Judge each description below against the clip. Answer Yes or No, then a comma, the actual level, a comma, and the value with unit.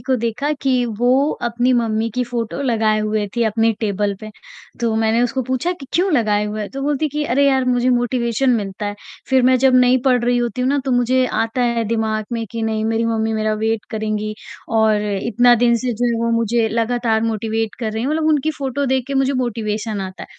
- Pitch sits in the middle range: No, high, 235 Hz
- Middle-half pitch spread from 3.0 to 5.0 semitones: No, narrow, 2.6 semitones